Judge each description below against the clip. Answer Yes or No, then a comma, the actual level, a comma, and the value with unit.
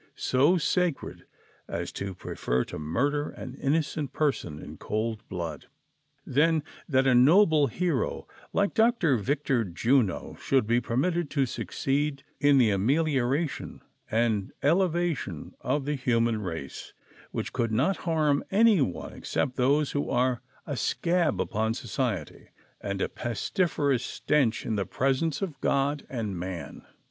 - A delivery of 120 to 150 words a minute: Yes, average, 140 wpm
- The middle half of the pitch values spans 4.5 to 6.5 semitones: Yes, average, 5.3 semitones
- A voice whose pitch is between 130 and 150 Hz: Yes, low, 135 Hz